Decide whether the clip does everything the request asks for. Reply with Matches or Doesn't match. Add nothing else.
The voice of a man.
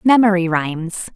Doesn't match